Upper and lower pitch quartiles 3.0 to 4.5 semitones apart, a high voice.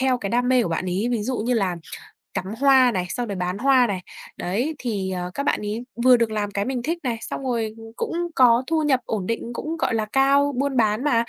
Yes: average, 4.2 semitones; high, 235 Hz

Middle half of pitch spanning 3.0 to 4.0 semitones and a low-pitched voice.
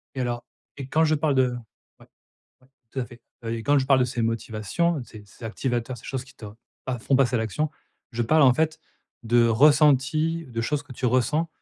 Yes: average, 3.7 semitones; low, 130 Hz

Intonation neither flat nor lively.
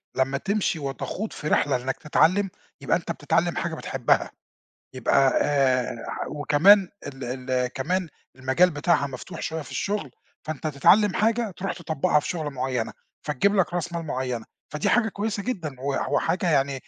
No: wide, 5.7 semitones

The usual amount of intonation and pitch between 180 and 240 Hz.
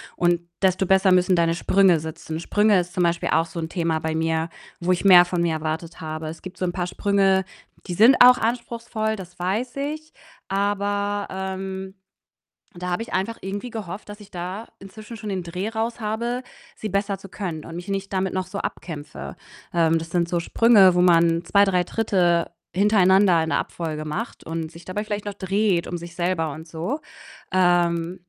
Yes: average, 3.1 semitones; medium, 185 Hz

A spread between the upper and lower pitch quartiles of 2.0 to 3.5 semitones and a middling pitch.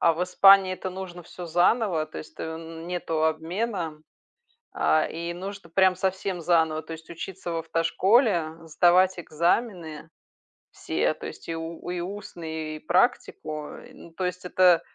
Yes: narrow, 2.5 semitones; medium, 170 Hz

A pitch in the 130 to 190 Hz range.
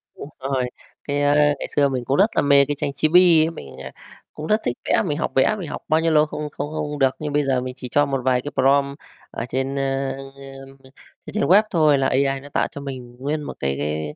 Yes: medium, 140 Hz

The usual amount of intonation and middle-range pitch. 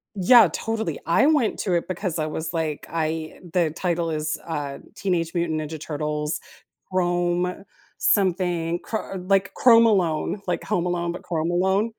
Yes: average, 3.0 semitones; medium, 175 Hz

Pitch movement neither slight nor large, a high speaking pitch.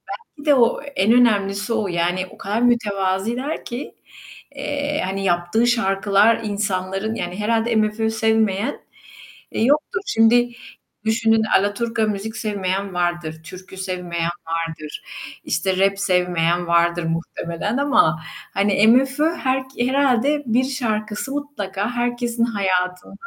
Yes: average, 4.5 semitones; high, 215 Hz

